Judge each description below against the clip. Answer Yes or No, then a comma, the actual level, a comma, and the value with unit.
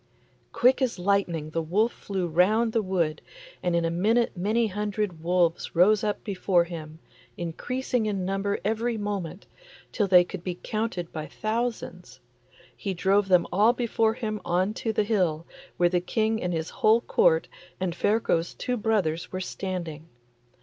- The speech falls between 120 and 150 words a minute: No, average, 160 wpm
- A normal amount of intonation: Yes, average, 4.0 semitones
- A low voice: No, high, 195 Hz